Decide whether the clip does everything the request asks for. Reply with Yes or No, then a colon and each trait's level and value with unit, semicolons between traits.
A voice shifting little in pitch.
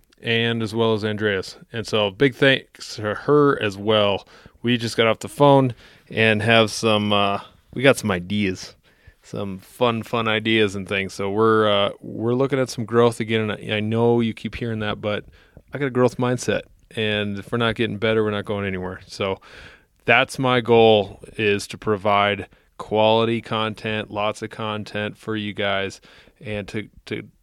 Yes: narrow, 2.1 semitones